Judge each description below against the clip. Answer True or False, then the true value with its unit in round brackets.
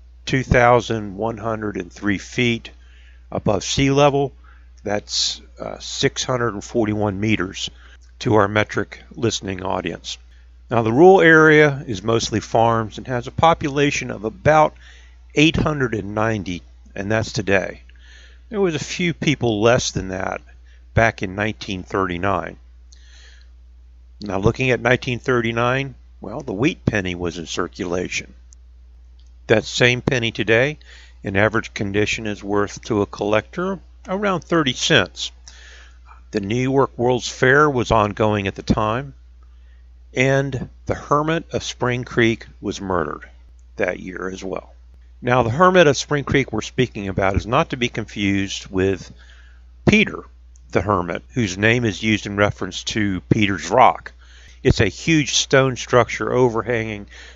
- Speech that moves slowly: True (130 wpm)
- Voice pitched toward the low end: True (105 Hz)